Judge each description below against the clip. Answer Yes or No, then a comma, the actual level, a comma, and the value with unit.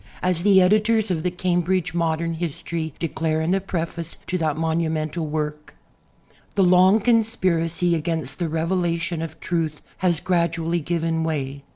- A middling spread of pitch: No, narrow, 2.1 semitones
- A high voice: No, medium, 170 Hz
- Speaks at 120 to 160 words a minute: Yes, average, 145 wpm